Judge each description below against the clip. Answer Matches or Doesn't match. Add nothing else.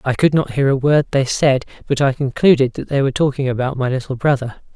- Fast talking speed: Matches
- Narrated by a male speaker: Matches